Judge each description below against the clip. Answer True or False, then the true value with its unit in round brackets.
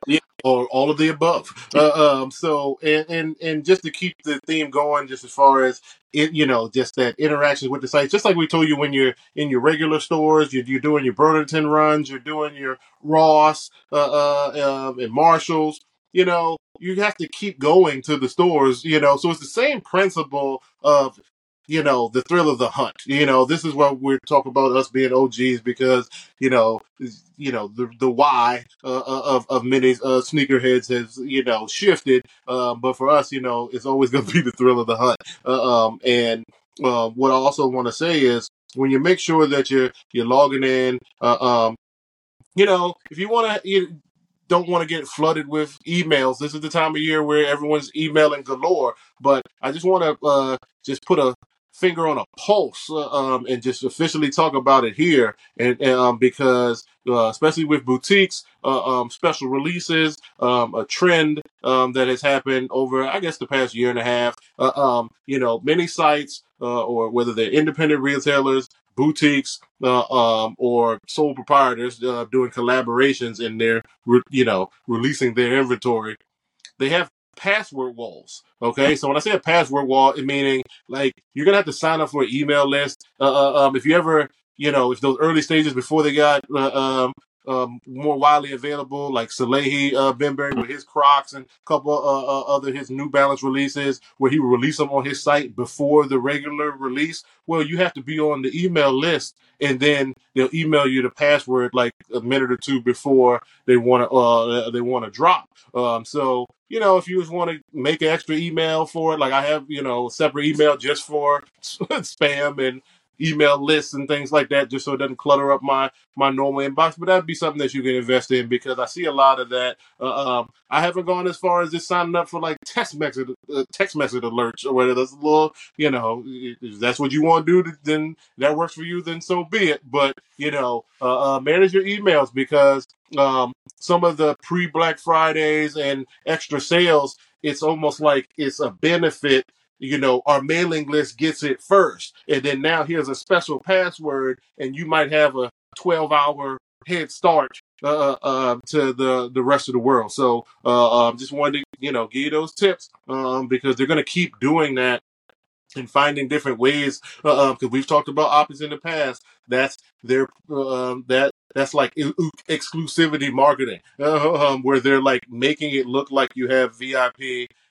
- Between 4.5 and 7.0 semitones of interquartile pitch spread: False (3.1 semitones)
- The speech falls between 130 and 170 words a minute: False (205 wpm)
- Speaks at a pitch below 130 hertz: False (140 Hz)